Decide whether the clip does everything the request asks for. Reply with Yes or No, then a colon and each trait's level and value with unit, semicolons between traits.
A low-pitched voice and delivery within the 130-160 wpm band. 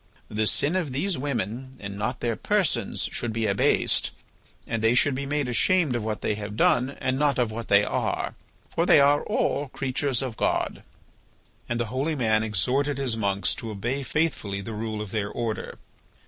No: low, 120 Hz; average, 190 wpm